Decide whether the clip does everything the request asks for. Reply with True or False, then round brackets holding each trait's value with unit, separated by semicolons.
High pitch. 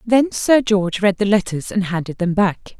True (200 Hz)